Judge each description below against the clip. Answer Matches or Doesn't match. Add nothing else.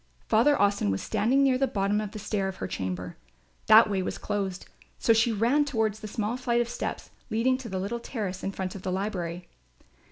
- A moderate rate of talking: Doesn't match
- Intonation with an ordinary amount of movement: Matches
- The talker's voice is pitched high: Matches